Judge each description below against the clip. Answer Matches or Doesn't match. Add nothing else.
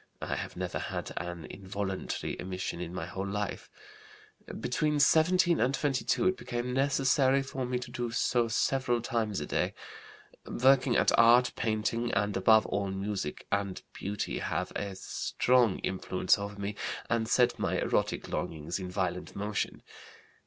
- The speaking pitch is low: Matches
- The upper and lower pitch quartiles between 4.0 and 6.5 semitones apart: Matches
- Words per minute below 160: Matches